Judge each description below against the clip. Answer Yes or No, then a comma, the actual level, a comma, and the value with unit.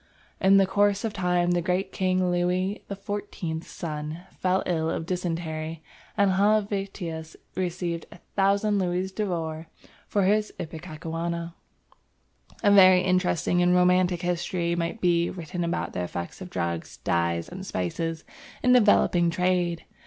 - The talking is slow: Yes, slow, 130 wpm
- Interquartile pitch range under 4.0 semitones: Yes, narrow, 2.4 semitones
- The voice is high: No, medium, 180 Hz